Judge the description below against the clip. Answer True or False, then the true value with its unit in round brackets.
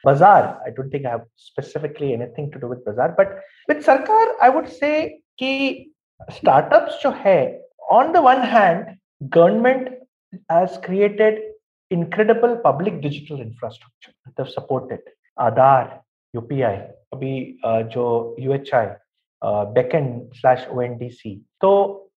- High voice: False (170 Hz)